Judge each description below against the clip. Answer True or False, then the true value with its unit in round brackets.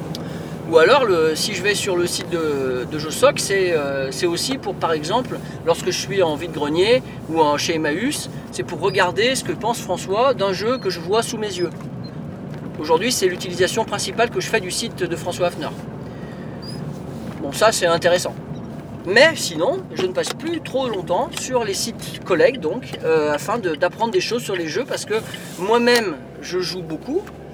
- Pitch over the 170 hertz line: True (185 Hz)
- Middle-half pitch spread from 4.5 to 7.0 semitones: True (5.3 semitones)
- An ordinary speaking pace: True (195 wpm)